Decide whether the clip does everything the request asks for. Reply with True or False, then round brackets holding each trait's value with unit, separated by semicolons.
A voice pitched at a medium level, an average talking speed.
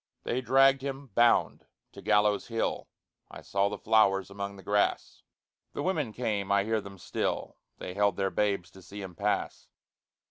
False (105 Hz; 170 wpm)